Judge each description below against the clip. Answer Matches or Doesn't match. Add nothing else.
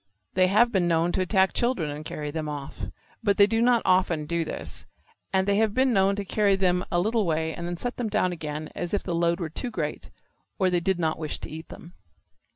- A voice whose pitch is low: Doesn't match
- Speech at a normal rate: Doesn't match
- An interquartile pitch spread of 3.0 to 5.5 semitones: Matches